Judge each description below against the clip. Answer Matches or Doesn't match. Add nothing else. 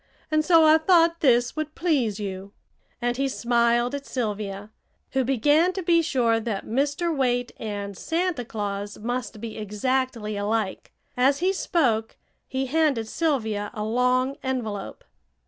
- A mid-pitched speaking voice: Doesn't match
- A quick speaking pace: Doesn't match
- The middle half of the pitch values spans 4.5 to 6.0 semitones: Matches